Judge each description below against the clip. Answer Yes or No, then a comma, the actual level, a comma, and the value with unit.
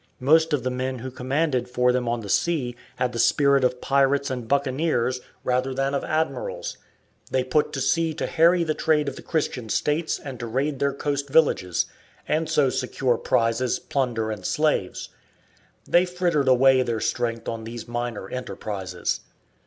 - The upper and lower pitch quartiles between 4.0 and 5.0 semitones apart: No, average, 3.5 semitones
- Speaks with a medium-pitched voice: No, low, 130 Hz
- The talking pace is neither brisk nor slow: Yes, average, 170 wpm